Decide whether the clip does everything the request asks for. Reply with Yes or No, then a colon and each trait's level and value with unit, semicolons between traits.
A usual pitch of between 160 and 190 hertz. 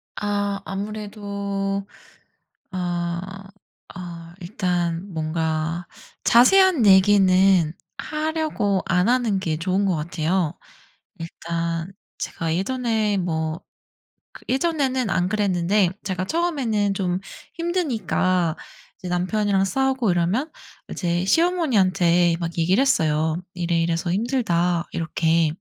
Yes: medium, 185 Hz